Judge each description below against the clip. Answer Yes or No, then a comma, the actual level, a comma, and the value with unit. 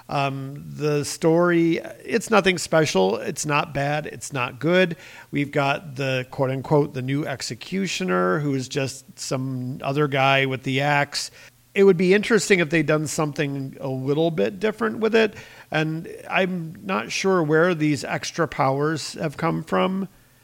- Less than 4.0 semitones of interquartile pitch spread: No, average, 4.4 semitones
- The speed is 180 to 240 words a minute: No, average, 160 wpm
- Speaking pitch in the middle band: Yes, medium, 150 Hz